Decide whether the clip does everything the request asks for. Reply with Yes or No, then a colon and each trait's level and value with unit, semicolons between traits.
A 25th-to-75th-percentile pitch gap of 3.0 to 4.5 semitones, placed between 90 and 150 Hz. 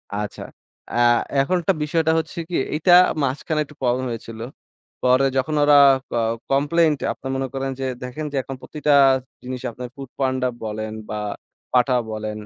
Yes: average, 3.4 semitones; low, 135 Hz